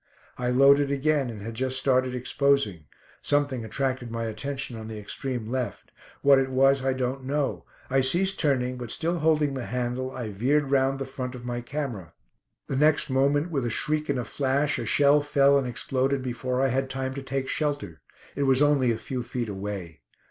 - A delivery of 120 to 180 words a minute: No, average, 195 wpm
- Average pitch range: No, narrow, 2.3 semitones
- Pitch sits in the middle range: No, low, 130 Hz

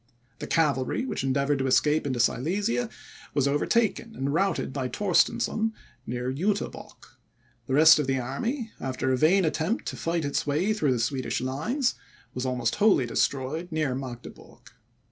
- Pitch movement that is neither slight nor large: No, wide, 6.8 semitones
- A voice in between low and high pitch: Yes, medium, 145 Hz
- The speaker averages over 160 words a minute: No, average, 155 wpm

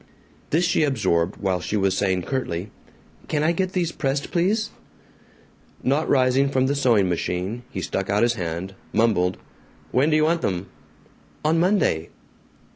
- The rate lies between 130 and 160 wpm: Yes, average, 155 wpm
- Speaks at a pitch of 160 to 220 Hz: No, low, 120 Hz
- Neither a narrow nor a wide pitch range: No, wide, 8.5 semitones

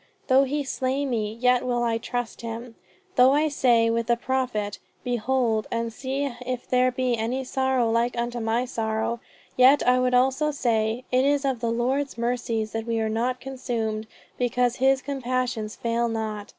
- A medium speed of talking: Yes, average, 175 wpm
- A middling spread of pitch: No, narrow, 2.3 semitones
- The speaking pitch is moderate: No, high, 245 Hz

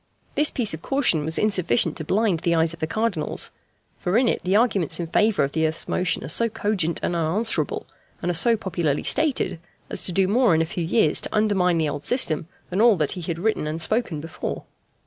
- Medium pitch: Yes, medium, 180 Hz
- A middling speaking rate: No, fast, 225 wpm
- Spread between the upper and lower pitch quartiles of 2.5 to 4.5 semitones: No, average, 5.1 semitones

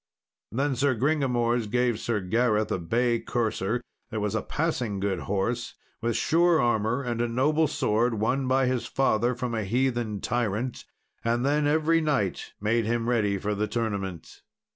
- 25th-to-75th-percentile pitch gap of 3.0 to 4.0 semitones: Yes, average, 3.4 semitones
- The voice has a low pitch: Yes, low, 120 Hz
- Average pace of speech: Yes, average, 165 wpm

